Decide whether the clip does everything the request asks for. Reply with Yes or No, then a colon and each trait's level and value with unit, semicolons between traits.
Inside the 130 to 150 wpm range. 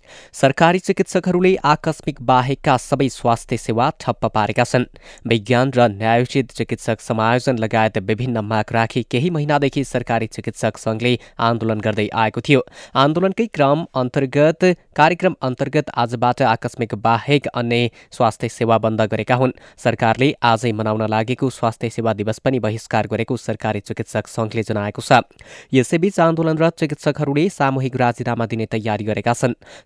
Yes: slow, 135 wpm